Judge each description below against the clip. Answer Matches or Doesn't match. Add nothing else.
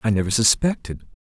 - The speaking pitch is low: Matches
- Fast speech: Doesn't match